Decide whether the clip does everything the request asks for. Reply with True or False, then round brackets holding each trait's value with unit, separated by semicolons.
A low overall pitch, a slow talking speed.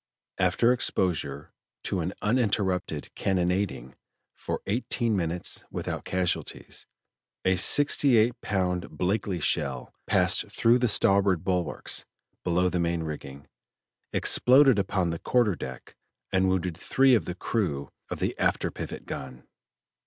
True (95 Hz; 125 wpm)